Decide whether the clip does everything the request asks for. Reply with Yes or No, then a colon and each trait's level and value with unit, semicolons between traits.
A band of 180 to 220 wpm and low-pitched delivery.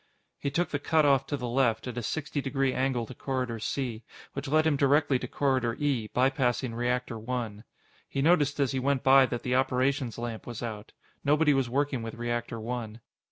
Yes: average, 200 wpm; low, 130 Hz